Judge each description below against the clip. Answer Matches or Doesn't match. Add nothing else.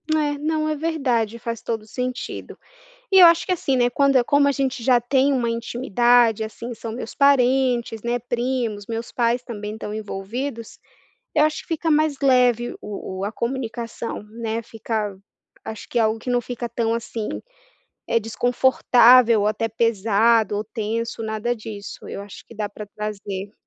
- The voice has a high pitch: Matches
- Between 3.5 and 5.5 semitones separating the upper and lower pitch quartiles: Doesn't match